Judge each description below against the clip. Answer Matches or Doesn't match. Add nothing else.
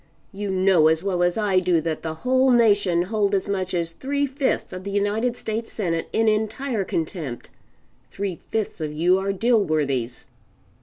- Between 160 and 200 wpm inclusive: Matches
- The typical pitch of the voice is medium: Doesn't match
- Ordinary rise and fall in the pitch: Matches